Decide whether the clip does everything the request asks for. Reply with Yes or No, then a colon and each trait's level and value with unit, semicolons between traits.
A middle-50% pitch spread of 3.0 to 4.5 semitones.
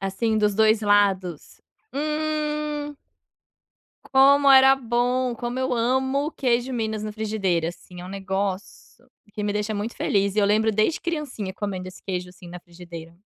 No: average, 5.2 semitones